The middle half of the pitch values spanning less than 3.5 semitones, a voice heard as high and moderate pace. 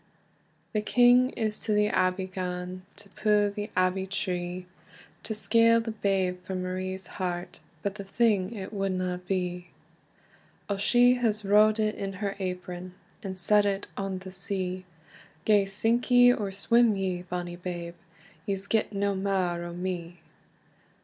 Yes: narrow, 2.4 semitones; high, 195 Hz; average, 150 wpm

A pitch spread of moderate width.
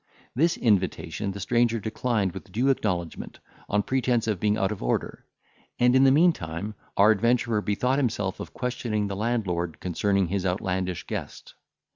Yes: average, 4.2 semitones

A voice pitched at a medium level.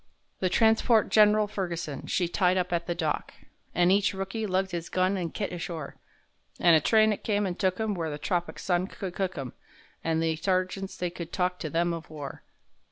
Yes: medium, 180 Hz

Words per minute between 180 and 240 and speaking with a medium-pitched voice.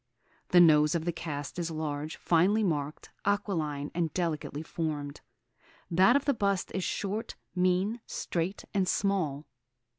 No: average, 140 wpm; medium, 170 Hz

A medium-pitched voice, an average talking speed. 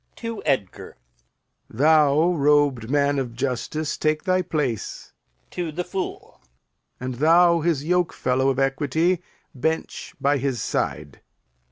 No: medium, 145 Hz; slow, 120 wpm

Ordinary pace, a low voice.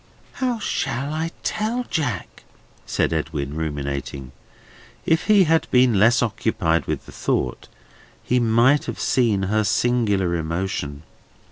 No: slow, 125 wpm; low, 110 Hz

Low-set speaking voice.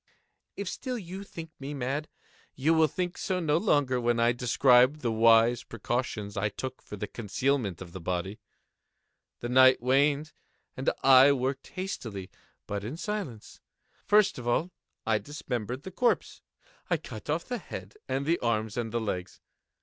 Yes: low, 130 Hz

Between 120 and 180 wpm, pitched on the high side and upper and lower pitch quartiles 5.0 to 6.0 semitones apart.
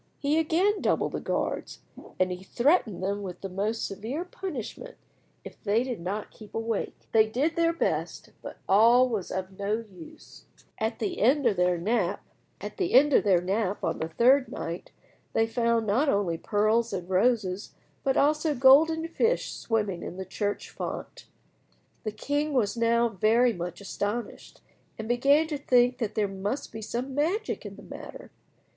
Yes: average, 160 wpm; high, 225 Hz; average, 5.3 semitones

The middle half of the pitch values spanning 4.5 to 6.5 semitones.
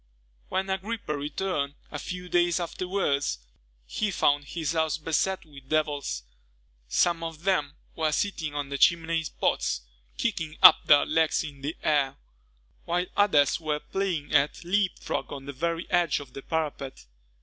No: average, 3.4 semitones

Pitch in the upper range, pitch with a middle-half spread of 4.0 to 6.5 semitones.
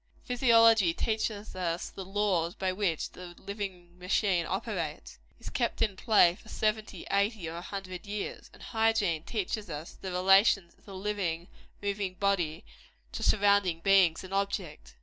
No: high, 195 Hz; average, 3.0 semitones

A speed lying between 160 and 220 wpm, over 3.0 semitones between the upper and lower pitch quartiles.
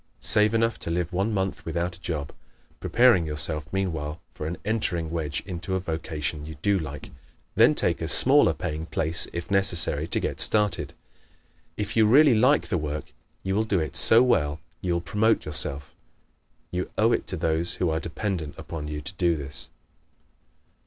Yes: average, 180 wpm; average, 4.4 semitones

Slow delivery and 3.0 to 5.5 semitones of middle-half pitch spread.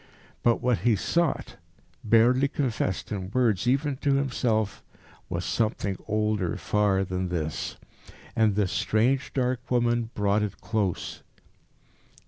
Yes: slow, 120 wpm; average, 3.8 semitones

